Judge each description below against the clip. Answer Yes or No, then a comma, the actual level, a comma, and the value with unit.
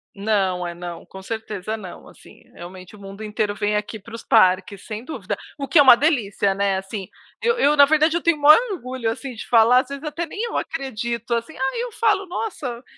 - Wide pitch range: Yes, wide, 6.4 semitones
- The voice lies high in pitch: Yes, high, 230 Hz